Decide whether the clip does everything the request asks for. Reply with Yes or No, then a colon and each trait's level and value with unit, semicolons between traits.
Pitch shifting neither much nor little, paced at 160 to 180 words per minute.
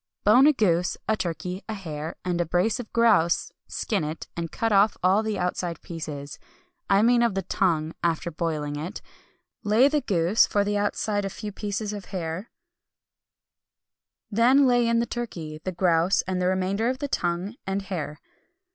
Yes: average, 4.3 semitones; average, 175 wpm